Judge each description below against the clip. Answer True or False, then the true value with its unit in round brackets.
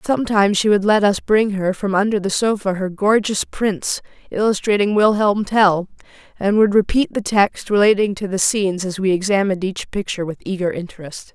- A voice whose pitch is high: True (200 Hz)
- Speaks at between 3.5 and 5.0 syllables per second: False (5.4 syllables/s)